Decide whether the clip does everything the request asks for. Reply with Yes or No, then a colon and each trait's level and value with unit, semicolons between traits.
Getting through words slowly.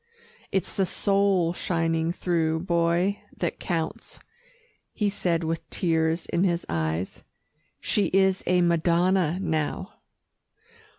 Yes: slow, 110 wpm